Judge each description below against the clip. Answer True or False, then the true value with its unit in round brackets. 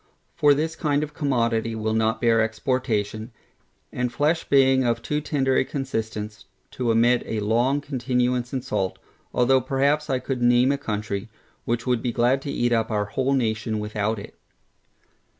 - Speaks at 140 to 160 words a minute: False (170 wpm)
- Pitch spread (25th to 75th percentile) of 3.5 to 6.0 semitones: False (3.1 semitones)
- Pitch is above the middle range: False (120 Hz)